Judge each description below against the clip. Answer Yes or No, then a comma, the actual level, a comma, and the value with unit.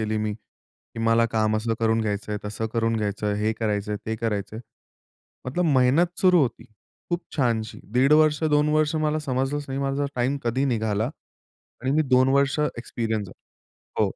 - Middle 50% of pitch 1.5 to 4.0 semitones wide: No, average, 4.5 semitones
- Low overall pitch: Yes, low, 115 Hz